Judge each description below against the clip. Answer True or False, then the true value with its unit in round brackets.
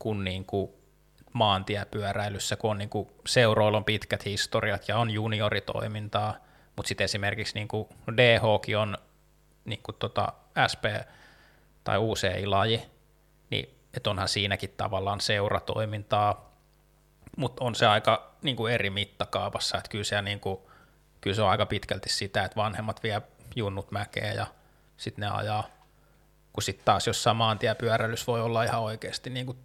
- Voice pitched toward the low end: True (105 Hz)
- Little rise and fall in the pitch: True (1.9 semitones)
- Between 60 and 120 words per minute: False (130 wpm)